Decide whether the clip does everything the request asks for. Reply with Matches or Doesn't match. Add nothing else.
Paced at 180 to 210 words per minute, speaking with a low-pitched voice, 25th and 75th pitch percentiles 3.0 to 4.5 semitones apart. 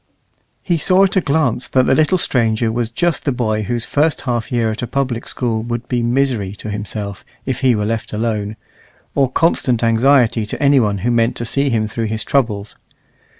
Matches